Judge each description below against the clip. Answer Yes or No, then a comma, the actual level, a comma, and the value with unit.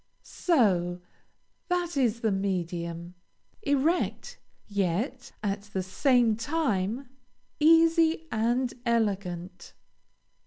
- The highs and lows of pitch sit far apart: Yes, wide, 7.2 semitones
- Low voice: No, high, 225 Hz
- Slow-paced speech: Yes, slow, 80 wpm